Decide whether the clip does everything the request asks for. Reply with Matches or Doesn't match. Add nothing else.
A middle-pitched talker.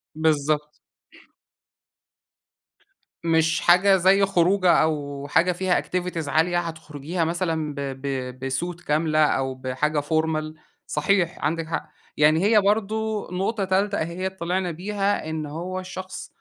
Matches